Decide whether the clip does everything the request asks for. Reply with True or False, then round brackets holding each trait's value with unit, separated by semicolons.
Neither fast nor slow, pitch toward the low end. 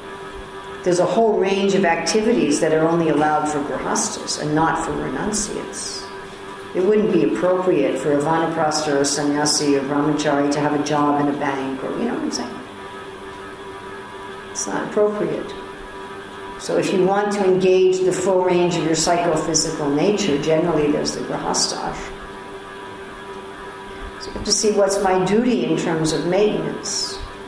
False (160 wpm; 145 Hz)